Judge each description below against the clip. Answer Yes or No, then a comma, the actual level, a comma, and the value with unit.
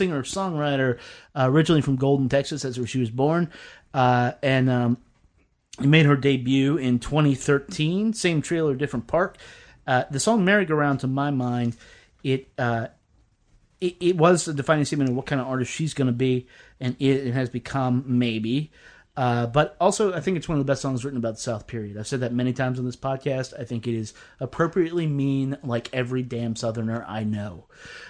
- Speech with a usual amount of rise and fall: Yes, average, 3.2 semitones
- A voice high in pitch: No, low, 135 Hz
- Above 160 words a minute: Yes, average, 190 wpm